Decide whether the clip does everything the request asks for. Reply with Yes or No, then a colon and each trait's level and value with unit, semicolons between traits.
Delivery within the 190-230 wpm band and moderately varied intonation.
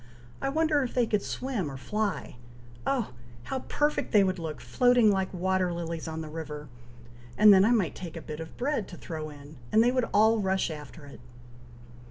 No: average, 200 wpm; wide, 6.6 semitones